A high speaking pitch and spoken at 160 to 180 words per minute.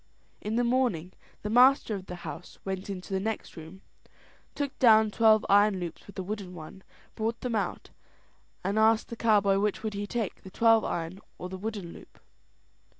No: high, 205 Hz; average, 195 wpm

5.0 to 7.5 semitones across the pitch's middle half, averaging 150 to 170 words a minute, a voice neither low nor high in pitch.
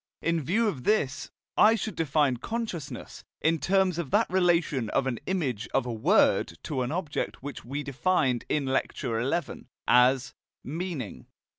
Yes: wide, 5.6 semitones; average, 155 wpm; medium, 150 Hz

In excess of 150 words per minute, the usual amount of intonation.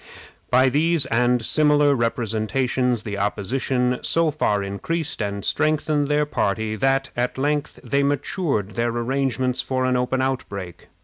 No: slow, 135 wpm; average, 4.1 semitones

